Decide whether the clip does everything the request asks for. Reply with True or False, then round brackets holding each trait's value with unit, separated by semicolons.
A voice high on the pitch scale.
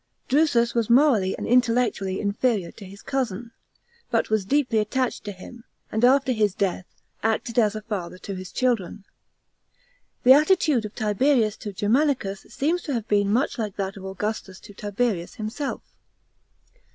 True (220 Hz)